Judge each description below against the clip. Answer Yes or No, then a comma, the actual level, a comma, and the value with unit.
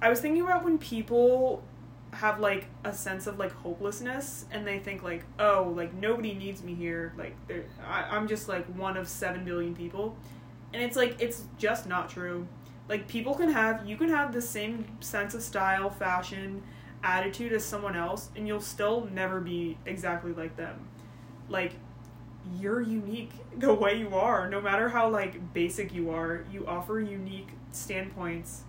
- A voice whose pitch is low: No, high, 195 Hz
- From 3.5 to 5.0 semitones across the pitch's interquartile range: Yes, average, 3.8 semitones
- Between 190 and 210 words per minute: No, average, 175 wpm